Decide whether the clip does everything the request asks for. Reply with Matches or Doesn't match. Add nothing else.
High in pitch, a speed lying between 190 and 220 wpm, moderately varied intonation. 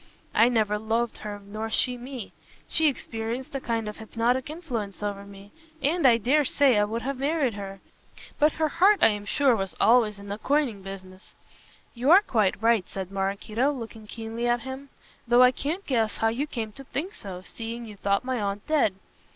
Matches